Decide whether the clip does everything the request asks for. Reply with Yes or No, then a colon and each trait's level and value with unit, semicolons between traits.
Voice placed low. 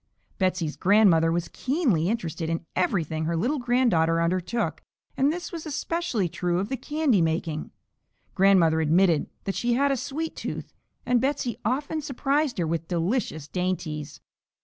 No: high, 190 Hz